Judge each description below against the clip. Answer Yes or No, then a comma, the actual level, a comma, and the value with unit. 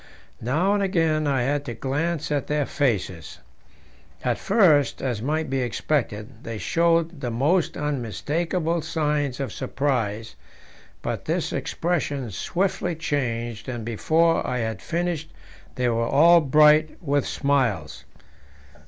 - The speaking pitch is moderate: Yes, medium, 145 Hz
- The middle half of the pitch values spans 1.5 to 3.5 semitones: No, average, 5.0 semitones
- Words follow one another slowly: Yes, slow, 125 wpm